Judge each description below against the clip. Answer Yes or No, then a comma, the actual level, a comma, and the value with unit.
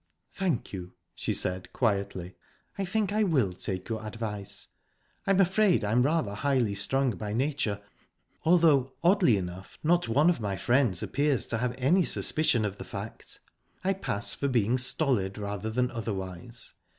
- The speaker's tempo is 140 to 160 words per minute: Yes, average, 155 wpm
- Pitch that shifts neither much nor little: No, wide, 6.9 semitones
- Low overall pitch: Yes, low, 120 Hz